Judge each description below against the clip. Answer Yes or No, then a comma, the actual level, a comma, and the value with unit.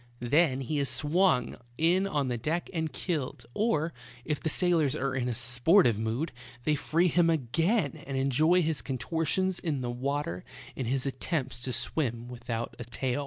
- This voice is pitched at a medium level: Yes, medium, 145 Hz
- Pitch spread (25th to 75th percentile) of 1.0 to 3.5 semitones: No, average, 4.8 semitones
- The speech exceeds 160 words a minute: Yes, average, 170 wpm